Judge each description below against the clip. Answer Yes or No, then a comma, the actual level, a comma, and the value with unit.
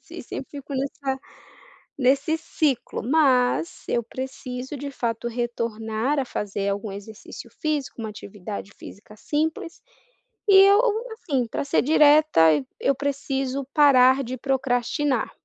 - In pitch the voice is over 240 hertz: Yes, very high, 260 Hz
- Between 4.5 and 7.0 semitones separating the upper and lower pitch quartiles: No, average, 4.0 semitones